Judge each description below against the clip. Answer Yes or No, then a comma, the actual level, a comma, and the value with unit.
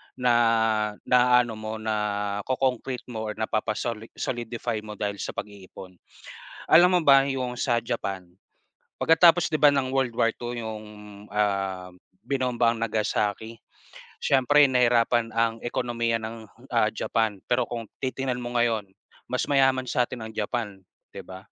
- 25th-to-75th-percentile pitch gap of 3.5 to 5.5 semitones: No, narrow, 2.6 semitones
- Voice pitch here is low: Yes, low, 115 Hz